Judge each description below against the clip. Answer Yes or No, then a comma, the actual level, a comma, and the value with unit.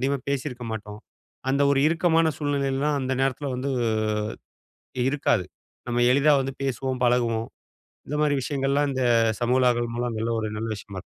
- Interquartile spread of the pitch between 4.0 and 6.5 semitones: No, average, 2.9 semitones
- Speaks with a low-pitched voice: Yes, low, 130 Hz